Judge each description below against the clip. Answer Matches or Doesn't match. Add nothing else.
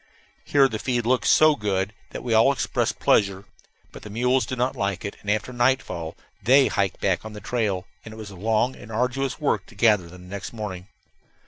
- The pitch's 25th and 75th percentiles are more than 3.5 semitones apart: Matches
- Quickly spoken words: Matches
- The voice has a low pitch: Matches